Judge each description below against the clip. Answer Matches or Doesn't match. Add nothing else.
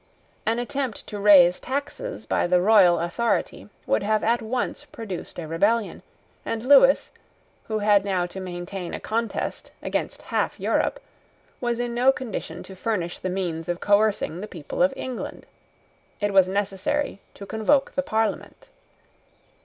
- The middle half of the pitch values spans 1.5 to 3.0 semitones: Doesn't match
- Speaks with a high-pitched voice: Matches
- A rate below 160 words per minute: Matches